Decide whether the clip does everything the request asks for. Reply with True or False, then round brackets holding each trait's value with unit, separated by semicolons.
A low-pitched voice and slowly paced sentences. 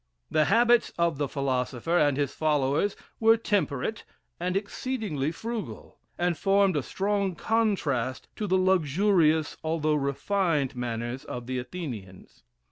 False (160 Hz; 125 wpm)